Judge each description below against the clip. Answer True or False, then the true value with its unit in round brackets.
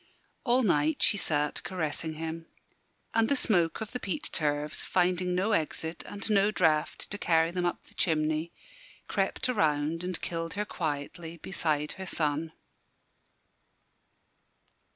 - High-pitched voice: False (165 Hz)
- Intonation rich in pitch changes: False (3.6 semitones)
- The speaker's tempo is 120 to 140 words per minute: True (135 wpm)